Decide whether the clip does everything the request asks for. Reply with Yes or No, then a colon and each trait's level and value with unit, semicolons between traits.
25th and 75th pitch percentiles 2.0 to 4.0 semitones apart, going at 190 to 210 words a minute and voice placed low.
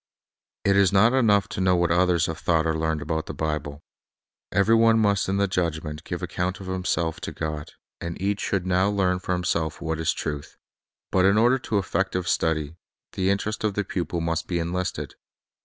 Yes: average, 3.3 semitones; average, 195 wpm; very low, 90 Hz